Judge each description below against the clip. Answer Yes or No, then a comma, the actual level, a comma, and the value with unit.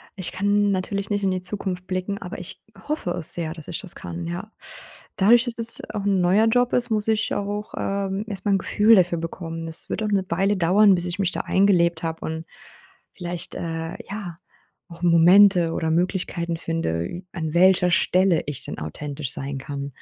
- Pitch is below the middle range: No, medium, 180 Hz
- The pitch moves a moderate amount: Yes, average, 3.3 semitones